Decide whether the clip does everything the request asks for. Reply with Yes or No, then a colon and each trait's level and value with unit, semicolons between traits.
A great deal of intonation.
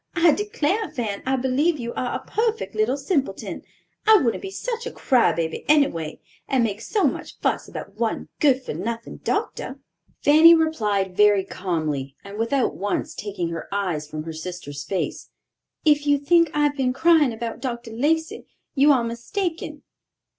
Yes: wide, 7.3 semitones